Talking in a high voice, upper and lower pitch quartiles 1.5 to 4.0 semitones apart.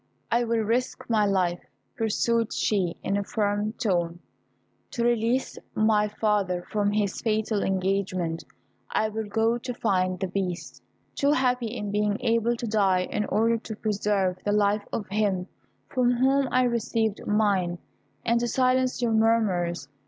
Yes: high, 215 Hz; average, 2.9 semitones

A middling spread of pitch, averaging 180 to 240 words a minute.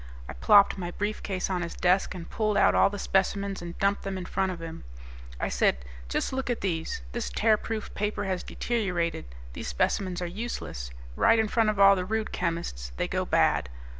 Yes: average, 3.4 semitones; average, 195 wpm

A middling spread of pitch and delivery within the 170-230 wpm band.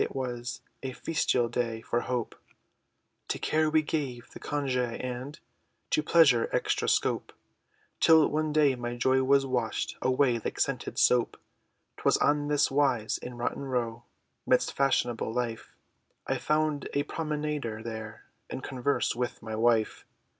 No: average, 3.5 semitones; average, 145 wpm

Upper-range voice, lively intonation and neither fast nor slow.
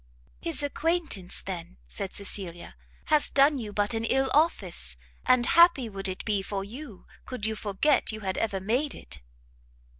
Yes: high, 220 Hz; wide, 6.4 semitones; average, 160 wpm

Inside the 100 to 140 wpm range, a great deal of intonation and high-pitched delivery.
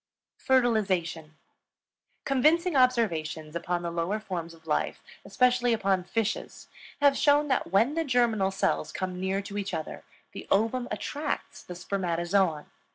Yes: slow, 135 wpm; wide, 6.4 semitones; high, 200 Hz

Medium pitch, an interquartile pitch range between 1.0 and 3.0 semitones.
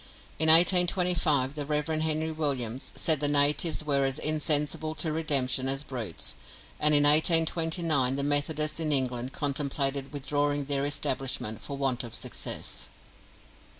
Yes: medium, 145 Hz; narrow, 2.4 semitones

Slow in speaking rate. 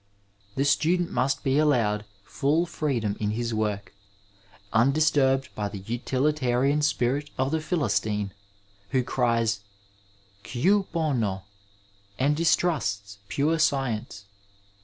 Yes: slow, 110 wpm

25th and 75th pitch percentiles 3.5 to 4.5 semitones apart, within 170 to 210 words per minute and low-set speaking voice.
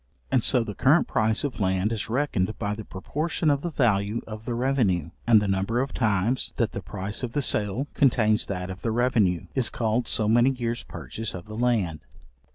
Yes: average, 3.8 semitones; fast, 205 wpm; low, 110 Hz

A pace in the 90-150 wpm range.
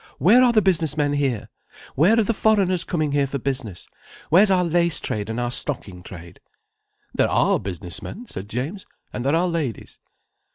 No: average, 180 wpm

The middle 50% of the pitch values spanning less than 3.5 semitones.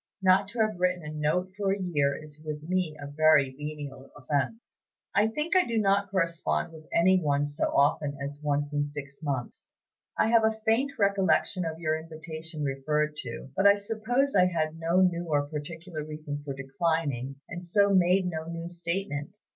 No: average, 4.3 semitones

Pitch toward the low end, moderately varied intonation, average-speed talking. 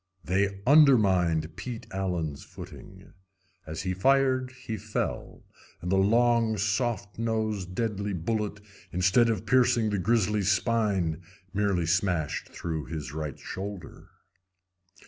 No: low, 100 Hz; average, 4.1 semitones; slow, 115 wpm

